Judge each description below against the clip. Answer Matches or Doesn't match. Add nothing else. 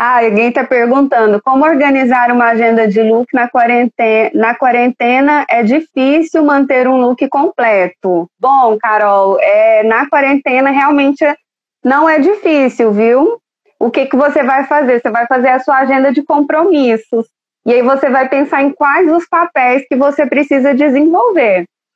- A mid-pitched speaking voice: Doesn't match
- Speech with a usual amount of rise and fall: Matches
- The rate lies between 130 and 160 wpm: Matches